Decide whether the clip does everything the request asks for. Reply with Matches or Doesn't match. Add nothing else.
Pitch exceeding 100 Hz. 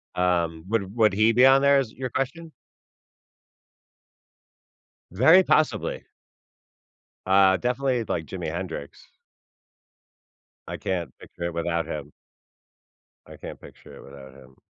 Doesn't match